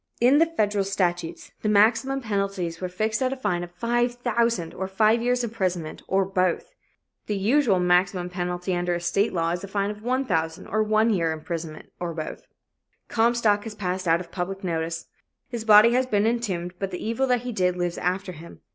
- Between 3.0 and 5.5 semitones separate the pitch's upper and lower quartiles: Yes, average, 4.5 semitones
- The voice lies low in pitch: No, high, 195 Hz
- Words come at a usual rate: Yes, average, 190 wpm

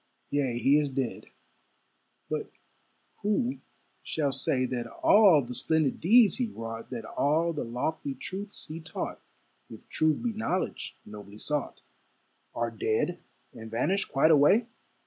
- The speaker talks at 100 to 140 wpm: Yes, slow, 135 wpm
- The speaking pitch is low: No, medium, 145 Hz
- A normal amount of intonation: No, wide, 6.7 semitones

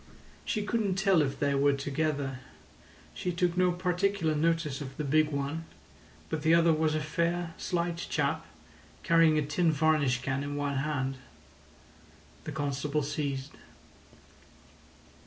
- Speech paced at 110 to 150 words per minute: Yes, average, 140 wpm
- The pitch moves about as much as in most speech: Yes, average, 3.1 semitones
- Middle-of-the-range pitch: Yes, medium, 155 Hz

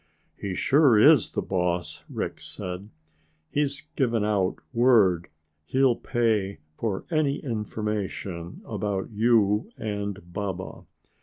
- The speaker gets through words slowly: Yes, slow, 105 wpm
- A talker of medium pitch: No, low, 105 Hz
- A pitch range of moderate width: Yes, average, 3.9 semitones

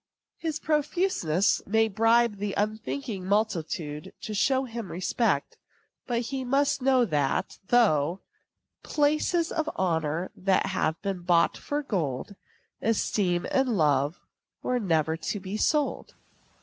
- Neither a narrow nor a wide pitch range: No, wide, 6.7 semitones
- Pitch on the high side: Yes, high, 210 Hz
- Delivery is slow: Yes, slow, 120 wpm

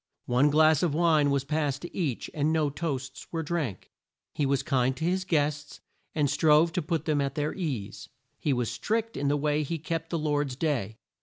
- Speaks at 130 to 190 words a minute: No, fast, 205 wpm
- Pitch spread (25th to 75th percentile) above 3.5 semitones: No, narrow, 2.6 semitones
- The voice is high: No, medium, 150 Hz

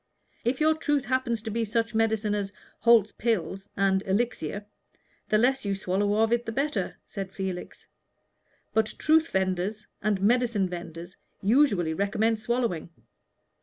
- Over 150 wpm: No, average, 140 wpm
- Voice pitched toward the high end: Yes, high, 215 Hz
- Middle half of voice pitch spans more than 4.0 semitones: No, average, 3.4 semitones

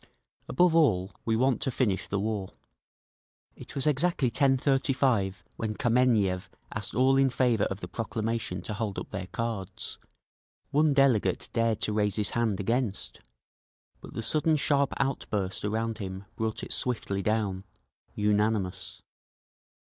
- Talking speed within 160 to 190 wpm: No, average, 140 wpm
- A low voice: Yes, low, 110 Hz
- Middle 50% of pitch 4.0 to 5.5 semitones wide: Yes, average, 4.5 semitones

